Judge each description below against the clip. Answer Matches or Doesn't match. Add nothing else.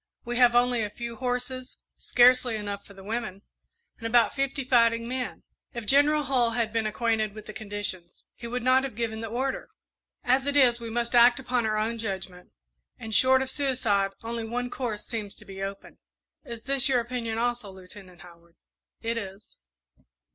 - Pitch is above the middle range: Matches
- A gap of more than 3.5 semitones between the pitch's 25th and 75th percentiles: Doesn't match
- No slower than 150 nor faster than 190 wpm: Matches